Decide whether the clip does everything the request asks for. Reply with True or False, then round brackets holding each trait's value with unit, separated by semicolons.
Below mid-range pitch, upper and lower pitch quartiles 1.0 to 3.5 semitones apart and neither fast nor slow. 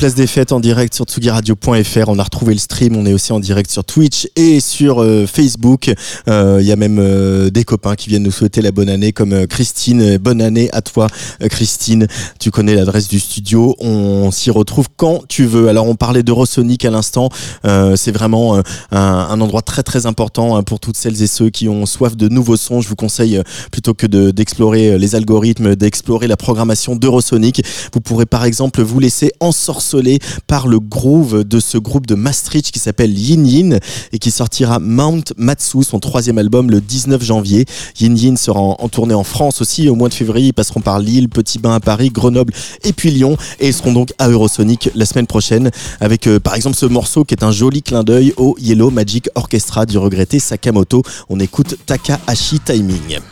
True (115 Hz; 3.0 semitones; 210 wpm)